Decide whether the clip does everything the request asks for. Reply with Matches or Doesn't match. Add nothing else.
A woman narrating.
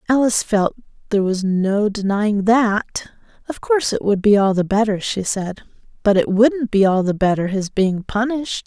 Matches